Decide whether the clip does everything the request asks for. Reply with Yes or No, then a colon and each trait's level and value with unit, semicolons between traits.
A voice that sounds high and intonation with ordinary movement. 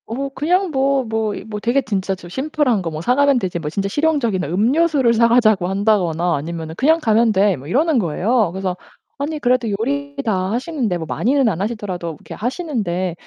No: high, 225 Hz; wide, 6.7 semitones